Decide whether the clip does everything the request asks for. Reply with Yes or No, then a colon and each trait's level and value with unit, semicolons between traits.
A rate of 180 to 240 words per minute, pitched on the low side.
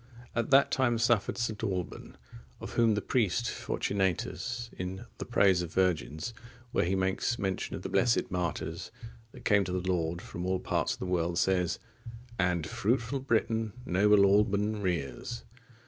No: average, 160 wpm; very low, 95 Hz